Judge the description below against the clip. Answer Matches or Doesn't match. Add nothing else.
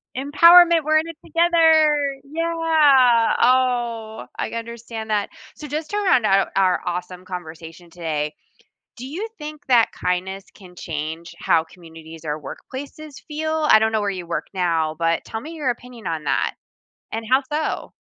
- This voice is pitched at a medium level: Doesn't match